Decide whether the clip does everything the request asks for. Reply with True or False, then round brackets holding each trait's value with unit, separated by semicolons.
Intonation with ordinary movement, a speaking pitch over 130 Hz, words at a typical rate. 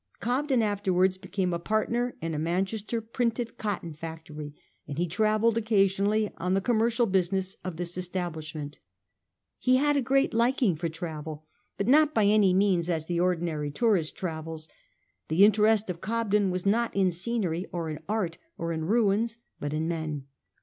True (4.9 semitones; 190 Hz; 170 wpm)